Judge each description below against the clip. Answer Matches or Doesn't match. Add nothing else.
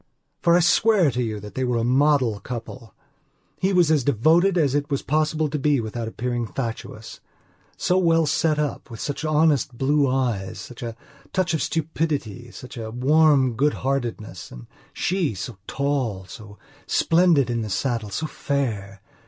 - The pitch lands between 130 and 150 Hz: Matches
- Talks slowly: Doesn't match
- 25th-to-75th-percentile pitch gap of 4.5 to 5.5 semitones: Matches